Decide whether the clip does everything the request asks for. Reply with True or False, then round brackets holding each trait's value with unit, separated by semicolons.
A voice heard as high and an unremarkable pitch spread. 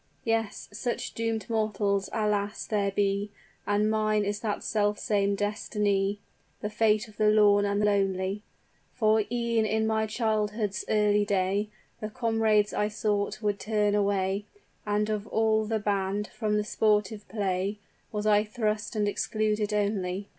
False (210 Hz; 1.1 semitones)